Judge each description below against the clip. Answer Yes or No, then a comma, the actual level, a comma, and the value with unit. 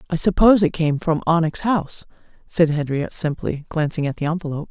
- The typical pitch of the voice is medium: Yes, medium, 160 Hz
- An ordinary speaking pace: Yes, average, 180 wpm